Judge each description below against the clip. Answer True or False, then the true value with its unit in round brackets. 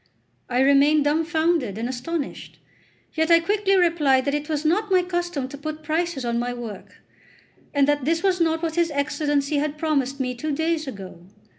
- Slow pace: False (180 wpm)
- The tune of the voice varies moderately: True (3.5 semitones)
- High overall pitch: True (300 Hz)